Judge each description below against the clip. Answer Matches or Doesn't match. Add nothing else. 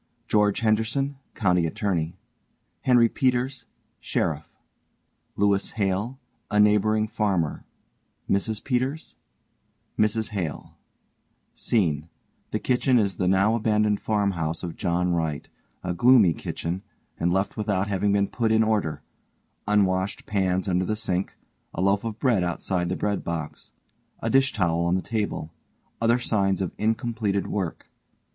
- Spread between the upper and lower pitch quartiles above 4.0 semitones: Doesn't match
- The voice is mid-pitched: Doesn't match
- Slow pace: Matches